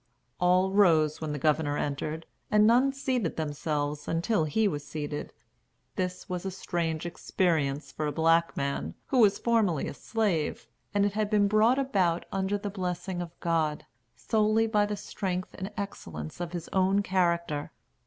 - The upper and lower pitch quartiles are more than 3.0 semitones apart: Yes, average, 4.6 semitones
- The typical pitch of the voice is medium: Yes, medium, 180 Hz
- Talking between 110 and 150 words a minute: No, average, 165 wpm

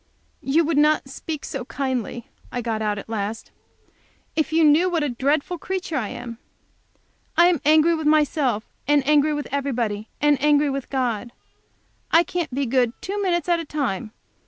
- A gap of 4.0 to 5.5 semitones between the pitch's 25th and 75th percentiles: Yes, average, 4.3 semitones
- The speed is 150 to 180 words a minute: Yes, average, 175 wpm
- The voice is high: Yes, very high, 285 Hz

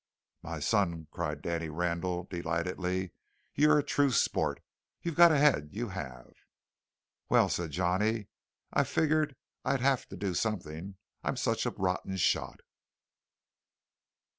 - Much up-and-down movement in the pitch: Yes, wide, 6.5 semitones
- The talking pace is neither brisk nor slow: No, slow, 130 wpm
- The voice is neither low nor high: No, very low, 95 Hz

